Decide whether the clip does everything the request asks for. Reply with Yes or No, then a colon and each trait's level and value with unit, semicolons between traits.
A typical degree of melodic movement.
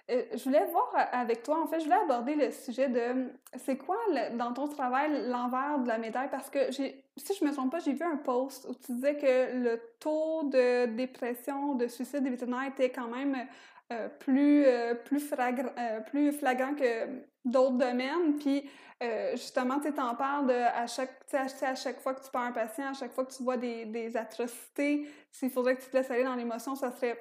No: narrow, 2.3 semitones